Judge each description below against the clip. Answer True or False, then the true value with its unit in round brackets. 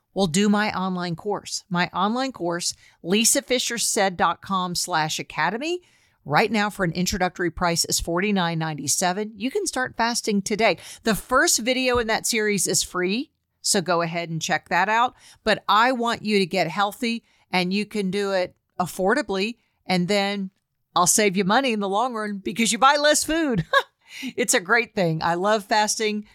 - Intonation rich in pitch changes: False (4.2 semitones)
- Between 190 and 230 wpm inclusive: False (170 wpm)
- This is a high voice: True (205 Hz)